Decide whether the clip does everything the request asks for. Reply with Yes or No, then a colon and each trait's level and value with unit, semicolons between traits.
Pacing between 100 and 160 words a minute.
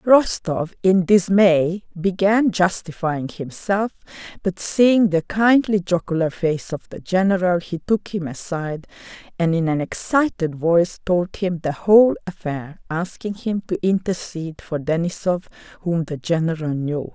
Yes: slow, 135 wpm